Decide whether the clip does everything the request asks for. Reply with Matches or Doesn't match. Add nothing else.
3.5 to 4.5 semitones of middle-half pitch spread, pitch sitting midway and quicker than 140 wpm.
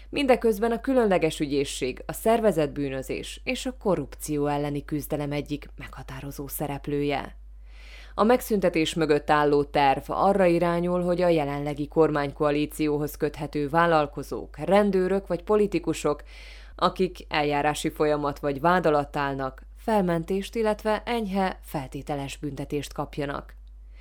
Doesn't match